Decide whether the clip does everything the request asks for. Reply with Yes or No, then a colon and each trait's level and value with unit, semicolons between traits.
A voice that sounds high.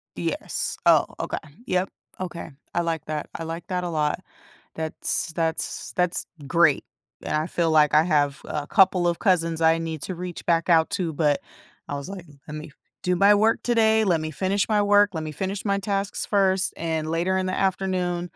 No: medium, 175 Hz